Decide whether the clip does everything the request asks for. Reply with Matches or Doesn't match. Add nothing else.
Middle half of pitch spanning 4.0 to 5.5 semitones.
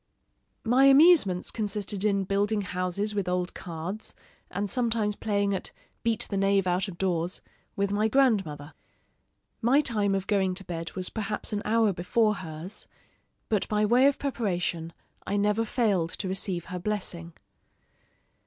Doesn't match